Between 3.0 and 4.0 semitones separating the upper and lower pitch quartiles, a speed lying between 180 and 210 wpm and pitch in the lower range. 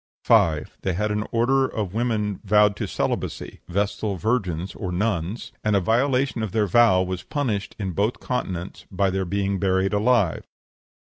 No: average, 3.3 semitones; average, 155 wpm; low, 100 Hz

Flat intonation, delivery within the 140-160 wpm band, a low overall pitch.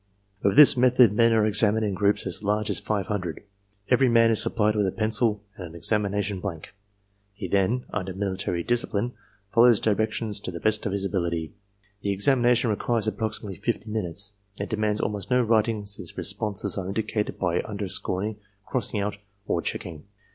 No: narrow, 2.2 semitones; average, 170 wpm; low, 105 Hz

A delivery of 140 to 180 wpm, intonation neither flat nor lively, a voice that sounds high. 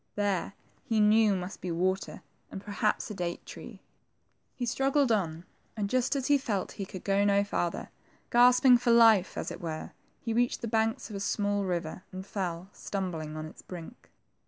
No: average, 190 wpm; average, 4.0 semitones; high, 200 Hz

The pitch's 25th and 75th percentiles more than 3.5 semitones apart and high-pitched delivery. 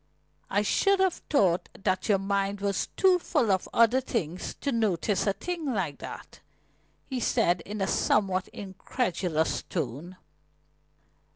Yes: average, 4.9 semitones; high, 200 Hz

